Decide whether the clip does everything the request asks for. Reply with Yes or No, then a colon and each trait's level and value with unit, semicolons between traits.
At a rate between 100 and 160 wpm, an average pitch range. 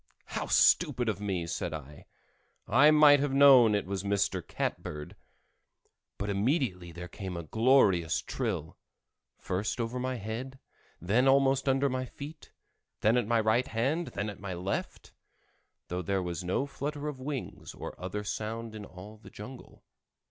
No: average, 155 wpm; wide, 5.8 semitones